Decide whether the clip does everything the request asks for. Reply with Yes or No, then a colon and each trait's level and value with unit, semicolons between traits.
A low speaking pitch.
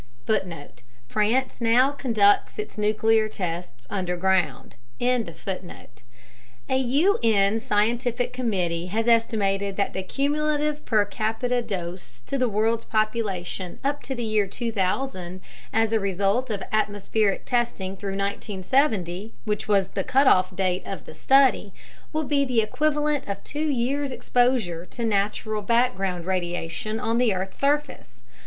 No: high, 215 Hz